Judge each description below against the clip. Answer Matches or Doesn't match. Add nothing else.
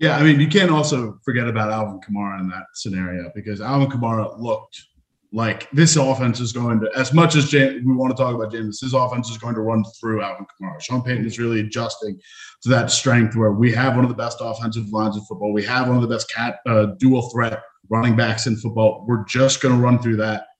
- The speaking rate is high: Matches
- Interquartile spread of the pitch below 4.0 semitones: Matches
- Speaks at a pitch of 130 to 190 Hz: Doesn't match